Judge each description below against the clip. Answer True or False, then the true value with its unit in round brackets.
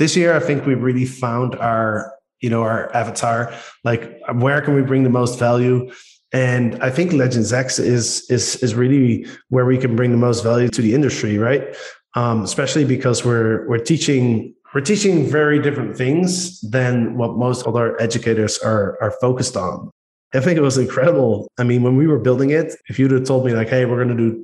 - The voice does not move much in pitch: True (2.3 semitones)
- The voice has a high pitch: False (125 Hz)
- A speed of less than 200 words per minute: False (205 wpm)